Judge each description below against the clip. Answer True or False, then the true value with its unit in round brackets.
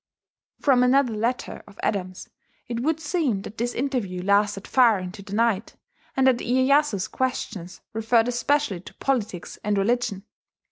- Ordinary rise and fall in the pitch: True (4.5 semitones)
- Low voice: False (230 Hz)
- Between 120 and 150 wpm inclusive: True (145 wpm)